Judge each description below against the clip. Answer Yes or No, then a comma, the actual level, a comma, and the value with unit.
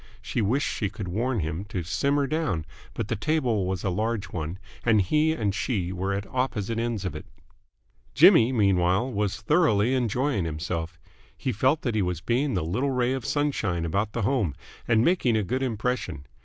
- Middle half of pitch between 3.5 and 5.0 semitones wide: No, wide, 5.5 semitones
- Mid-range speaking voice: No, low, 110 Hz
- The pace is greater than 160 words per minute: Yes, average, 185 wpm